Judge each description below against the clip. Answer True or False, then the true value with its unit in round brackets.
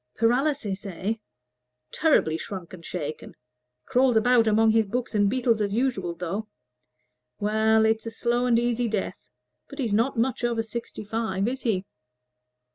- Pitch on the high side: True (225 Hz)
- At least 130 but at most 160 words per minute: True (150 wpm)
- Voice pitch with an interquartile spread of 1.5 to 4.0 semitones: True (3.0 semitones)